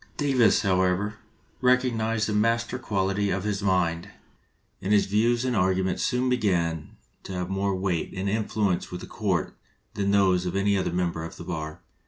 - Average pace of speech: Yes, average, 170 wpm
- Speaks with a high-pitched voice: No, low, 100 Hz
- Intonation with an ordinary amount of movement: Yes, average, 3.0 semitones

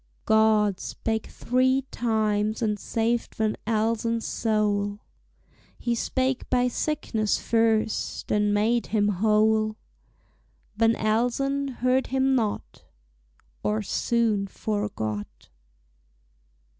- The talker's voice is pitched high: Yes, high, 220 Hz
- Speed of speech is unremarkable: No, slow, 95 wpm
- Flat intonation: Yes, narrow, 2.2 semitones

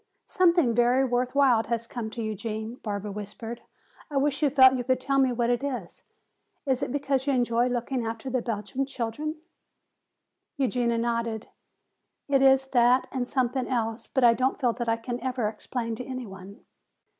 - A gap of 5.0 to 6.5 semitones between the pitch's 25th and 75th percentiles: No, narrow, 2.5 semitones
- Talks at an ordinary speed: Yes, average, 180 wpm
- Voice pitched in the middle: No, high, 245 Hz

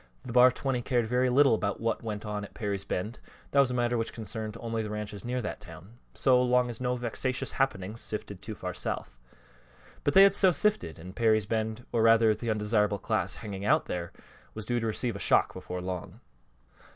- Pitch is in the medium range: No, low, 115 Hz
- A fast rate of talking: Yes, fast, 210 wpm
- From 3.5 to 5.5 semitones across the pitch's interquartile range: No, average, 3.1 semitones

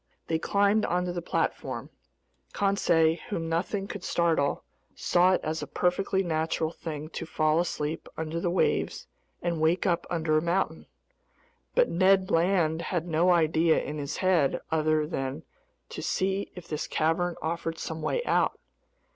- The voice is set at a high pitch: No, medium, 170 Hz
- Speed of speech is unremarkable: Yes, average, 155 wpm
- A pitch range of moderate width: No, narrow, 2.3 semitones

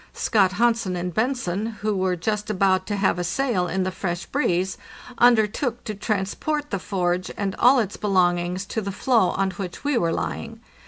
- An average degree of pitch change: Yes, average, 3.6 semitones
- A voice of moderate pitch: No, high, 200 Hz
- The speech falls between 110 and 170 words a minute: No, average, 180 wpm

